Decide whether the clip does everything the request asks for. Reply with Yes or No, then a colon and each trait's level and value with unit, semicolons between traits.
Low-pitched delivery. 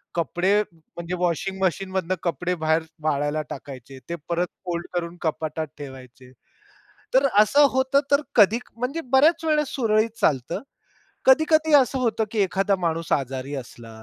No: medium, 180 Hz